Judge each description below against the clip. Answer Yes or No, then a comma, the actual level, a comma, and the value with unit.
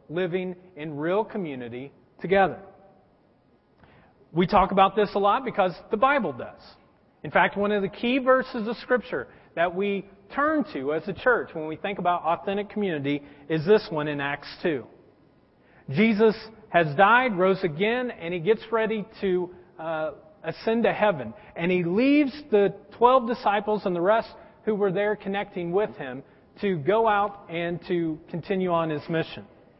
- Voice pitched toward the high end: Yes, high, 195 Hz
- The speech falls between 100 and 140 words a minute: No, average, 165 wpm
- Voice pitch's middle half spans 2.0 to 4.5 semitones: Yes, average, 4.0 semitones